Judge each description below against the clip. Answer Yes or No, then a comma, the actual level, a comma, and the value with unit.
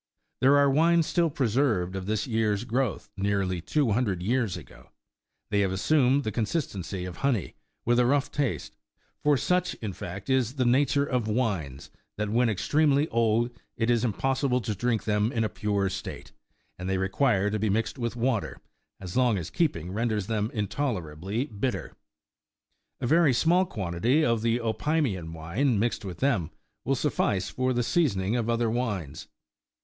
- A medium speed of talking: Yes, average, 165 wpm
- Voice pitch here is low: Yes, low, 115 Hz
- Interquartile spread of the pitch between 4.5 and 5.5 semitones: Yes, average, 5.0 semitones